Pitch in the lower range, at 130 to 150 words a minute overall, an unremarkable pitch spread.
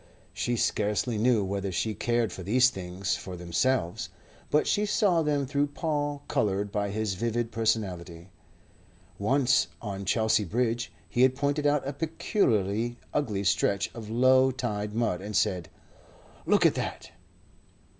Yes: low, 110 Hz; average, 145 wpm; average, 4.7 semitones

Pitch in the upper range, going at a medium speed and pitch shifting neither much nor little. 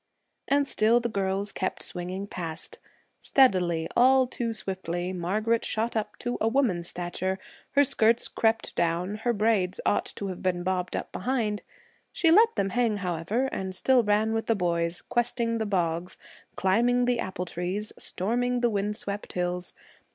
Yes: high, 205 Hz; average, 160 wpm; average, 4.6 semitones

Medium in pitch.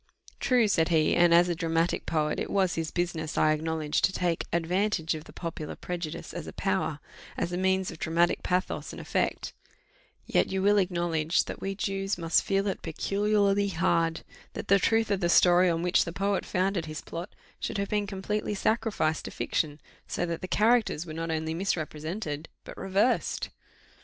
Yes: medium, 175 Hz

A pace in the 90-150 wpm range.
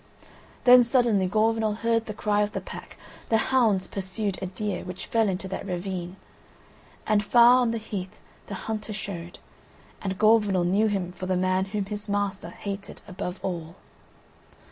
No: average, 165 wpm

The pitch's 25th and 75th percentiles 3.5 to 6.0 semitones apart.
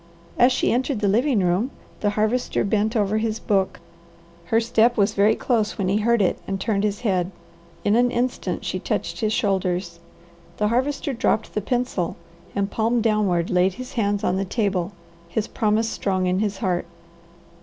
No: average, 3.0 semitones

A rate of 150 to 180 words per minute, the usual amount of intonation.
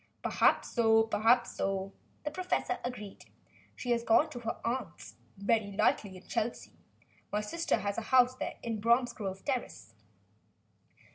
No: average, 140 wpm; average, 3.4 semitones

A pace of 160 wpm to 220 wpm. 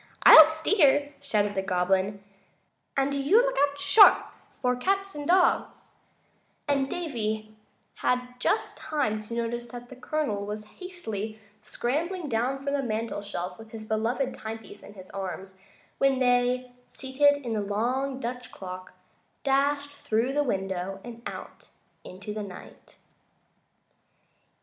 No: average, 140 wpm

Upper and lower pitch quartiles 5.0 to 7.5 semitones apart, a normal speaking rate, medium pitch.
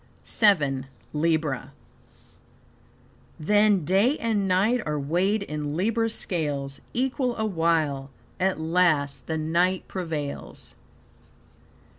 No: wide, 5.4 semitones; slow, 90 wpm; medium, 170 Hz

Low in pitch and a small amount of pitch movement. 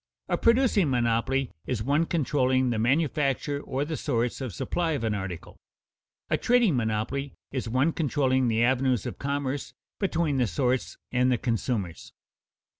No: low, 130 Hz; average, 3.6 semitones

